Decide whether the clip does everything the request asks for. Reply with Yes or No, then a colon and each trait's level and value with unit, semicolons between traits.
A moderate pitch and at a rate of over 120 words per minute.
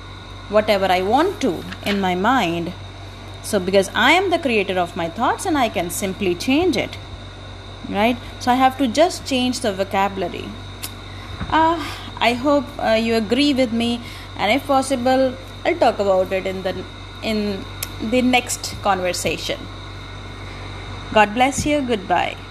No: high, 195 Hz; average, 150 wpm